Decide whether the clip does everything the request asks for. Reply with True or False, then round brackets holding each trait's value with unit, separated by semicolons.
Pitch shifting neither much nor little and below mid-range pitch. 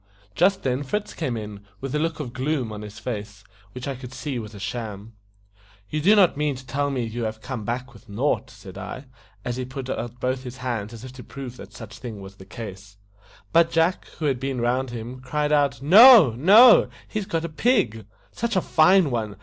True (4.9 semitones; 130 Hz)